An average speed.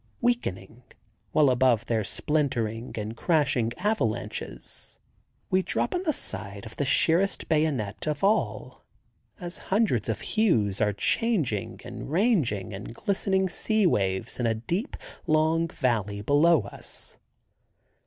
No: slow, 125 wpm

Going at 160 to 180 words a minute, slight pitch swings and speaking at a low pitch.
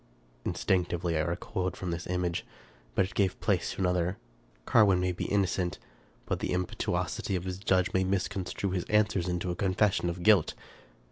Yes: average, 165 wpm; narrow, 1.4 semitones; very low, 90 Hz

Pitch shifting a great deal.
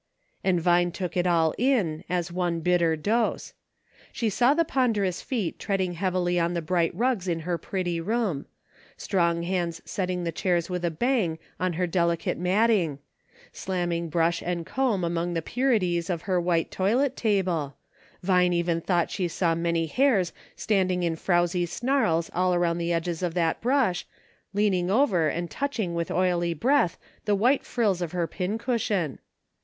No: average, 3.0 semitones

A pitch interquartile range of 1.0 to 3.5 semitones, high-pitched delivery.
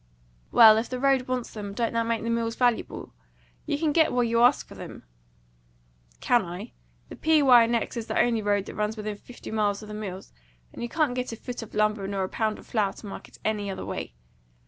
Yes: narrow, 2.6 semitones; high, 230 Hz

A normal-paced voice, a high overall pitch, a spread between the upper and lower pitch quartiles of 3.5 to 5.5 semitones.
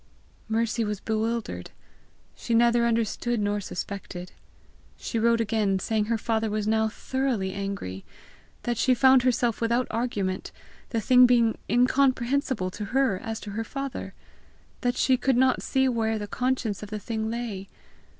No: average, 150 wpm; high, 225 Hz; average, 2.9 semitones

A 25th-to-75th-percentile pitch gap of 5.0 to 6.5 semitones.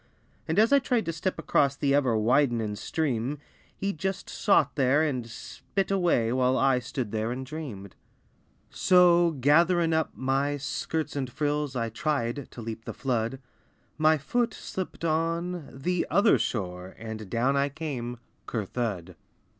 Yes: wide, 5.4 semitones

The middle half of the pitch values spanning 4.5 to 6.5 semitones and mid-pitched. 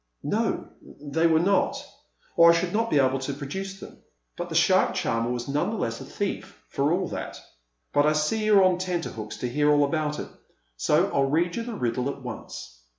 Yes: average, 5.2 semitones; medium, 150 Hz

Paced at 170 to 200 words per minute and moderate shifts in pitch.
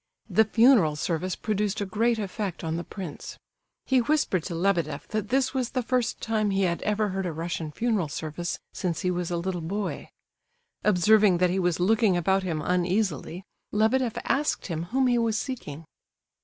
Yes: average, 180 wpm; average, 4.2 semitones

